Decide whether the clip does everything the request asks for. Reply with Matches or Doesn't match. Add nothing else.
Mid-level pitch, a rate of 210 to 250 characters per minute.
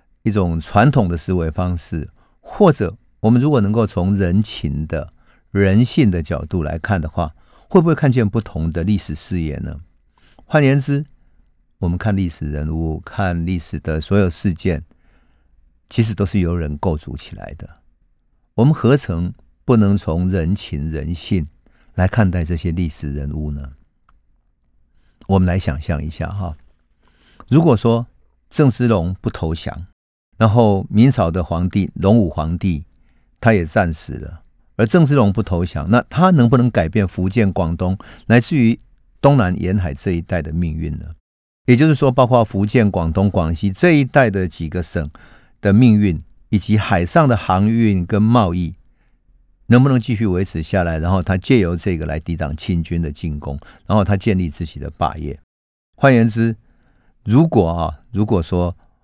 Doesn't match